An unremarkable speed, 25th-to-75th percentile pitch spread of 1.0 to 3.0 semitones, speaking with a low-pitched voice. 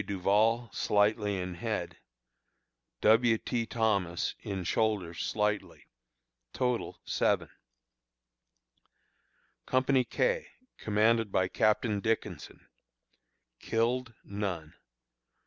No: slow, 80 wpm; average, 2.7 semitones; low, 110 Hz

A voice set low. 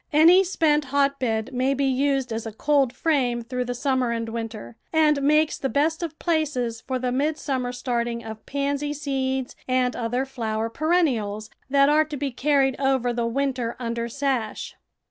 No: very high, 265 Hz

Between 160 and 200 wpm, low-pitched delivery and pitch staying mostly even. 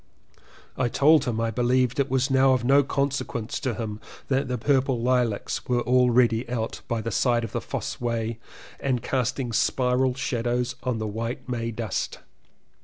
Yes: average, 180 wpm; low, 125 Hz; narrow, 2.2 semitones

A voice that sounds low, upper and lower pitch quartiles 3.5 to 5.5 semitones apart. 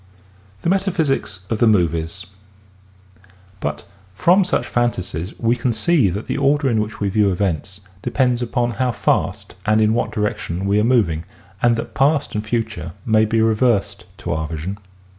Yes: low, 110 Hz; average, 4.1 semitones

